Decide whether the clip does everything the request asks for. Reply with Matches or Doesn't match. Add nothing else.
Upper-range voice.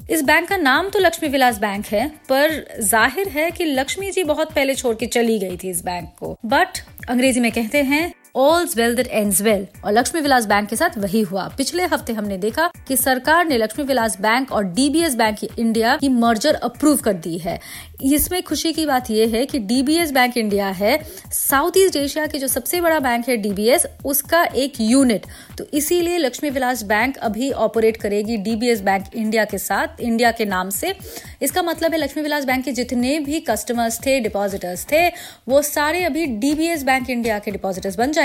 Matches